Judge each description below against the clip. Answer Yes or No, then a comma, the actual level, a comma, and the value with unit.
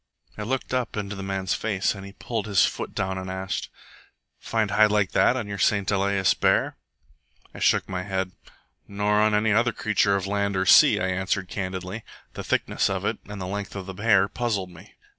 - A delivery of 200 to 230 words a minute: Yes, fast, 205 wpm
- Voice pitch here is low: Yes, low, 100 Hz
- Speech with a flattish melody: Yes, narrow, 1.9 semitones